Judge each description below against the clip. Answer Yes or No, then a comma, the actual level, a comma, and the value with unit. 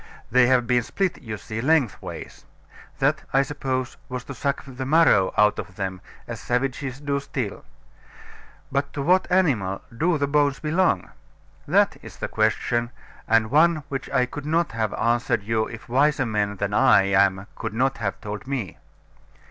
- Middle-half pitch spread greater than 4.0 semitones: Yes, average, 4.6 semitones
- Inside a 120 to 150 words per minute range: No, average, 165 wpm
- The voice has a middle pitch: No, low, 125 Hz